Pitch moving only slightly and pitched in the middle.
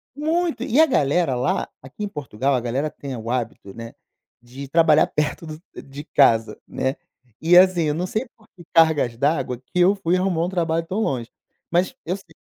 No: wide, 5.6 semitones; medium, 160 Hz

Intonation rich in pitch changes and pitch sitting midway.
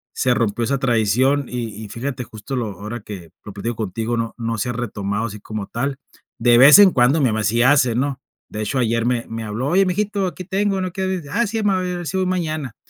No: wide, 6.0 semitones; low, 125 Hz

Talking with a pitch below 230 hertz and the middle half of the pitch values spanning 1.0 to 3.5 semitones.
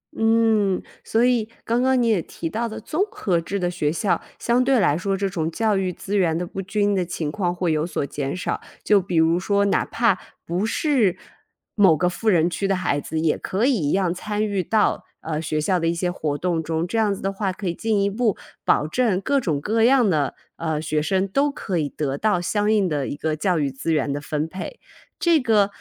No: medium, 185 Hz; average, 4.8 semitones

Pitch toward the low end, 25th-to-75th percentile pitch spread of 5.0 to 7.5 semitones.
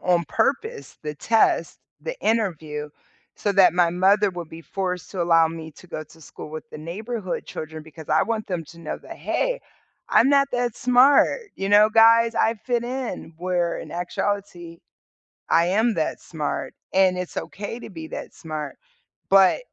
No: medium, 185 Hz; wide, 5.4 semitones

